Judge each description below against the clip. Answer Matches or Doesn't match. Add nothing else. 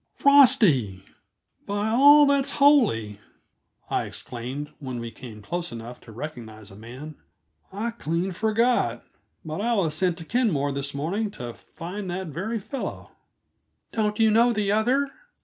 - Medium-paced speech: Matches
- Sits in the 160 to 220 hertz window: Matches